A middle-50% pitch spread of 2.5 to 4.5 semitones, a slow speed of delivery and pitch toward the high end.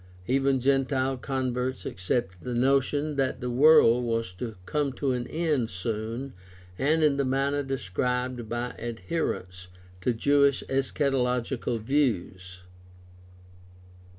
No: average, 2.8 semitones; slow, 115 wpm; low, 130 Hz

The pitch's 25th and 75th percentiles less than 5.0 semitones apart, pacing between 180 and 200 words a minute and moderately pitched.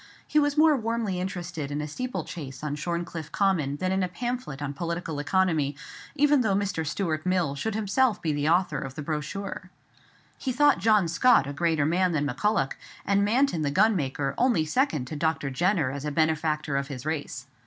No: wide, 5.4 semitones; average, 185 wpm; medium, 170 Hz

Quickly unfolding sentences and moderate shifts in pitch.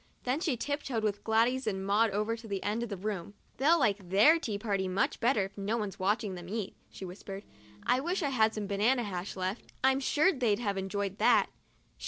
Yes: fast, 225 wpm; average, 3.8 semitones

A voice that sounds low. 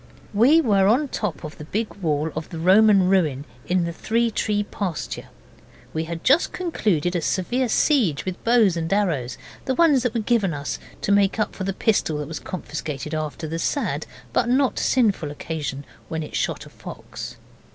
No: high, 190 Hz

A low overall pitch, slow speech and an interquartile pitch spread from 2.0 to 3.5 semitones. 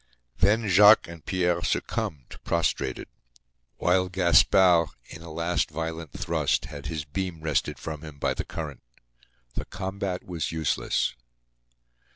Yes: very low, 85 Hz; slow, 130 wpm; average, 2.7 semitones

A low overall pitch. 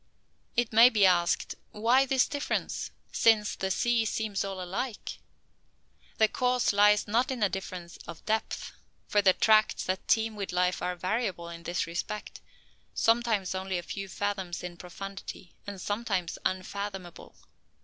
No: high, 200 Hz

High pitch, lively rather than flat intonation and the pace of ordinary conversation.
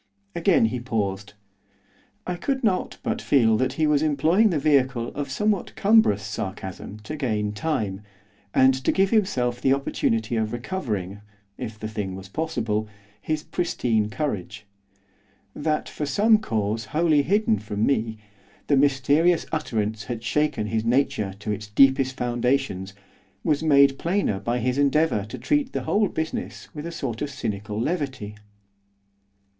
No: low, 130 Hz; wide, 6.4 semitones; average, 150 wpm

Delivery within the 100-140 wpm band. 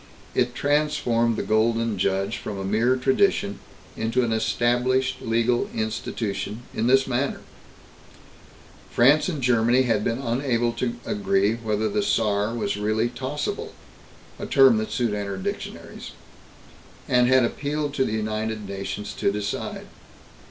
Yes: slow, 135 wpm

